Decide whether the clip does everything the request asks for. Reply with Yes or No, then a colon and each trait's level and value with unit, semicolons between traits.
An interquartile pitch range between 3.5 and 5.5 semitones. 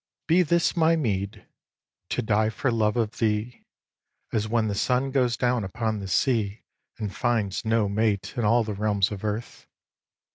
No: average, 2.7 semitones